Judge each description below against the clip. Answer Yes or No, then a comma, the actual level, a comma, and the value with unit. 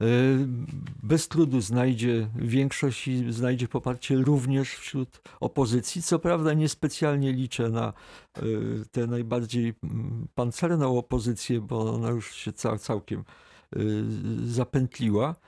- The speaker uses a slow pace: Yes, slow, 95 wpm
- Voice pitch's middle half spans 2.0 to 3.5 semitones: Yes, average, 2.9 semitones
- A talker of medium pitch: No, low, 125 Hz